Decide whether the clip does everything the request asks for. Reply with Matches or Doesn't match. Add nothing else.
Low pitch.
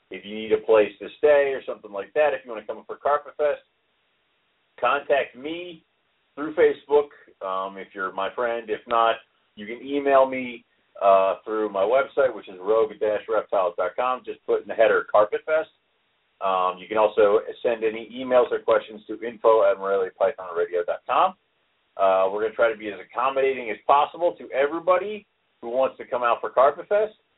Doesn't match